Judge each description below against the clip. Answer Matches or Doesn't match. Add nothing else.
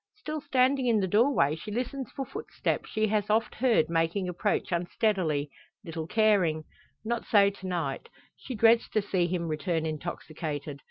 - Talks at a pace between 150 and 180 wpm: Matches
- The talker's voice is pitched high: Matches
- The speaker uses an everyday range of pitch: Doesn't match